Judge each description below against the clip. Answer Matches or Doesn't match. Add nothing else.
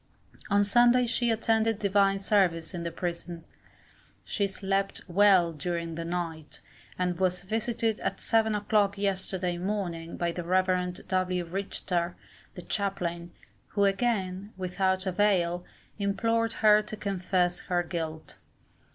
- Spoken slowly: Matches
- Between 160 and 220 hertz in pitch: Matches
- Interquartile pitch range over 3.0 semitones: Doesn't match